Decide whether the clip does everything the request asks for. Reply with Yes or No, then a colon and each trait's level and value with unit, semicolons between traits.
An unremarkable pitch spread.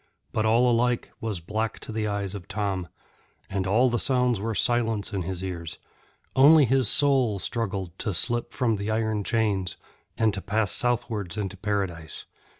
Yes: average, 3.5 semitones